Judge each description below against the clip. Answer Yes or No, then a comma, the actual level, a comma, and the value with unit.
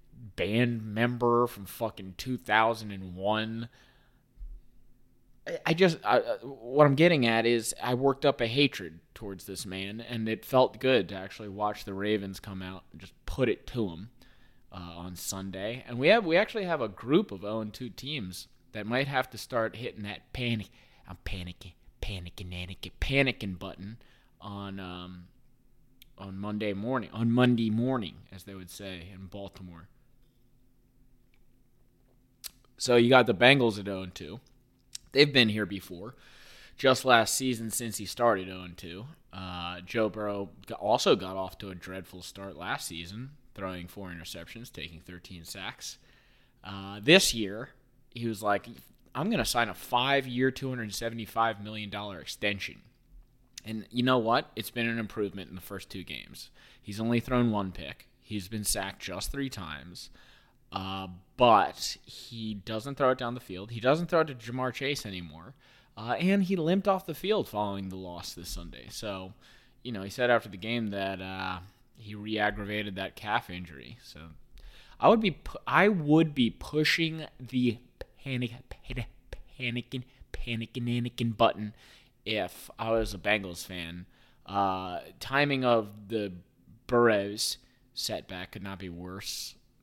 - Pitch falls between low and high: No, low, 110 Hz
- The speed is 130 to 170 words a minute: Yes, average, 160 wpm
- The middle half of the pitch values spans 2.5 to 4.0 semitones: No, average, 4.7 semitones